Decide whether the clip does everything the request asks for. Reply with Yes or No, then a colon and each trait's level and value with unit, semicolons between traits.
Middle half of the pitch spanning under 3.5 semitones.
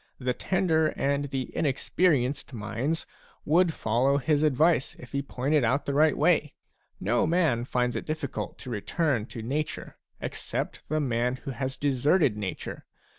No: average, 3.8 semitones